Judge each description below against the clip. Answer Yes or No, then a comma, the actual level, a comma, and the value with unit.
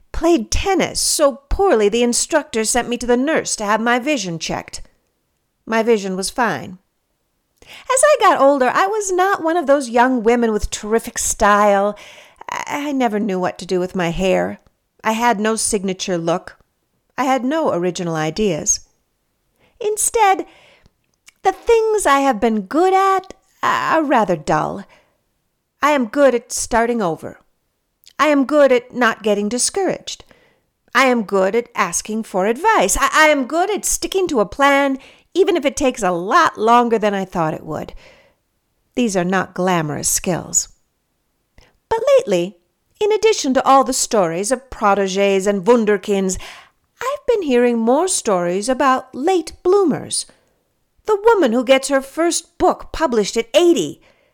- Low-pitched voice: No, high, 245 Hz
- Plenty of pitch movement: Yes, wide, 7.7 semitones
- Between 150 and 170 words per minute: Yes, average, 155 wpm